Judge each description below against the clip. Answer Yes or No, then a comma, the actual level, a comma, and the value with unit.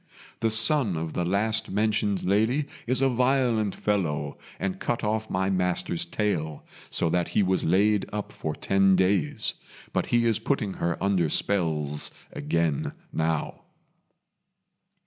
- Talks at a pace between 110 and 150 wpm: Yes, average, 140 wpm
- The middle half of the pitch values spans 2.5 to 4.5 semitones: Yes, average, 4.2 semitones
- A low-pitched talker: Yes, low, 100 Hz